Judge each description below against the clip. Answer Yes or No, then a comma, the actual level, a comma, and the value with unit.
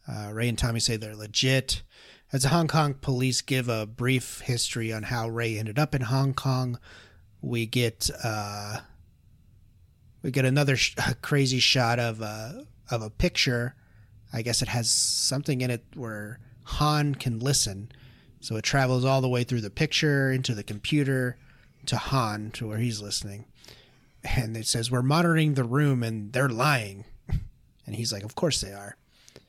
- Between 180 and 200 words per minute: No, average, 170 wpm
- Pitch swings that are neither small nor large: Yes, average, 3.4 semitones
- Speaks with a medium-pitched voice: No, low, 120 Hz